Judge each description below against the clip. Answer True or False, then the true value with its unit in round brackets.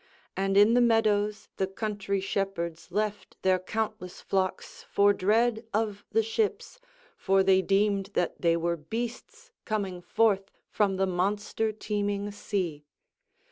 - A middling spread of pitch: False (2.3 semitones)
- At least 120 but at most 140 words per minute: True (135 wpm)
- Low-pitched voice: False (200 Hz)